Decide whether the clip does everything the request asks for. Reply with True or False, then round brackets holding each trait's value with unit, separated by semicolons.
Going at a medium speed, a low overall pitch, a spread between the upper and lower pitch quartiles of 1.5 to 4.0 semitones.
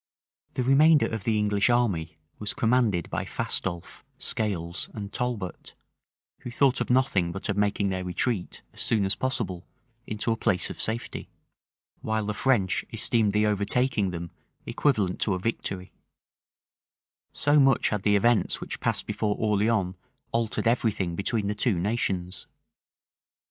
True (150 wpm; 105 Hz; 3.7 semitones)